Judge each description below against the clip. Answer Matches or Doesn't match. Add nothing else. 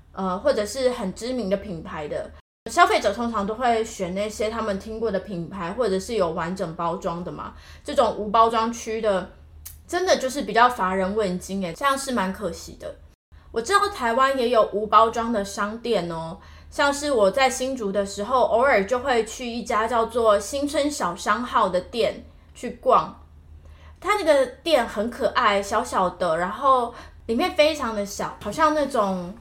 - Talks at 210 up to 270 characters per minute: Matches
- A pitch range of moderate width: Matches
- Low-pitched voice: Doesn't match